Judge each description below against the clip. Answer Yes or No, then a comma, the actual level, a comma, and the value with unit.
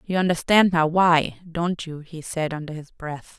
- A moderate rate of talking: Yes, average, 175 wpm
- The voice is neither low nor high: Yes, medium, 165 Hz